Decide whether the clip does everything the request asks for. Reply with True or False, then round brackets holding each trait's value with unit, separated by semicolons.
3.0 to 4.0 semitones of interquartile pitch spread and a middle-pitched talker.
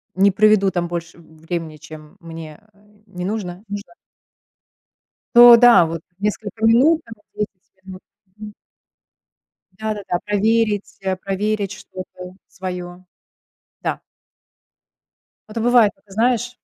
False (3.4 semitones; 200 Hz)